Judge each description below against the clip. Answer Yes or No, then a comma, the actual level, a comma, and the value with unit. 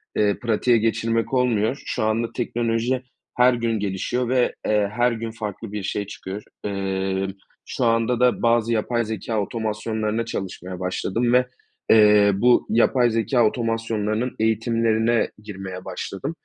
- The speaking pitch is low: Yes, low, 115 Hz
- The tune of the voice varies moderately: No, narrow, 2.2 semitones